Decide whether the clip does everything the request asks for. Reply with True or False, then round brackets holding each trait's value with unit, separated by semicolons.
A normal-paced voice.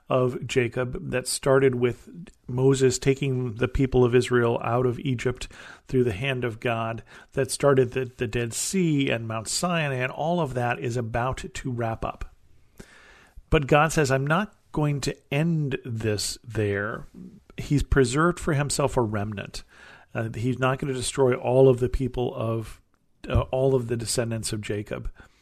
True (170 wpm)